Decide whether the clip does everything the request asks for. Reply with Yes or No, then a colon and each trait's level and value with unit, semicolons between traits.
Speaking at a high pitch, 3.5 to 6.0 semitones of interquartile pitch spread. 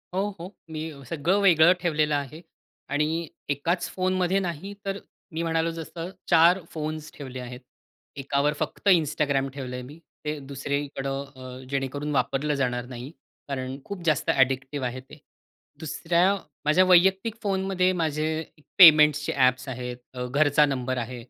No: medium, 150 Hz; average, 4.0 semitones